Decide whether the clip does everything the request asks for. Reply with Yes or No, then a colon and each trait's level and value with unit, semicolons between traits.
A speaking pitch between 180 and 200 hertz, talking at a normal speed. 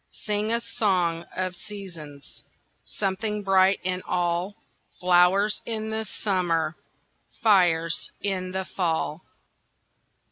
No: medium, 185 Hz; slow, 100 wpm